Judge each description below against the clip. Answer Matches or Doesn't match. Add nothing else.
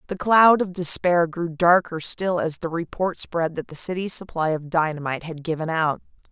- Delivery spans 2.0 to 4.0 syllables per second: Doesn't match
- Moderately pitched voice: Matches